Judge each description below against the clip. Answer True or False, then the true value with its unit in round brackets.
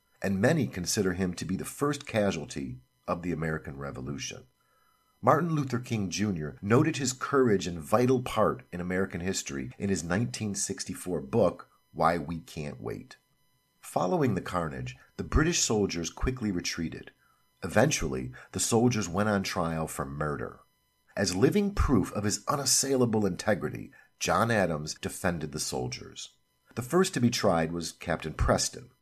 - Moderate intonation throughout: False (6.2 semitones)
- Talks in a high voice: False (90 Hz)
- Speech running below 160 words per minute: True (145 wpm)